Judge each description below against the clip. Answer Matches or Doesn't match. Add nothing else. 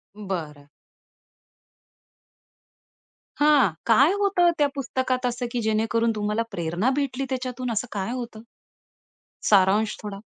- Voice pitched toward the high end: Matches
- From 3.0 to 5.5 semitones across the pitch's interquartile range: Matches